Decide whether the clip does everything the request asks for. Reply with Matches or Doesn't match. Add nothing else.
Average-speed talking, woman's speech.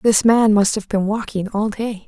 Doesn't match